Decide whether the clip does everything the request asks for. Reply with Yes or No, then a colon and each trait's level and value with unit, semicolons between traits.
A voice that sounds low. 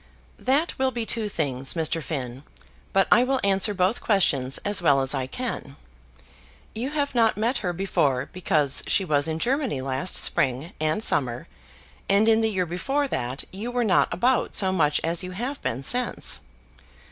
No: medium, 185 Hz